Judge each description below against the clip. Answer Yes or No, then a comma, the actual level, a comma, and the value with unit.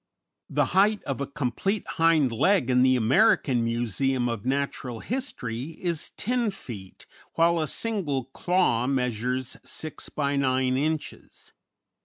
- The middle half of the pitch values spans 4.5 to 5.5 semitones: Yes, average, 5.1 semitones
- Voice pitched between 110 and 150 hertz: Yes, low, 135 Hz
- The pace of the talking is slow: Yes, slow, 130 wpm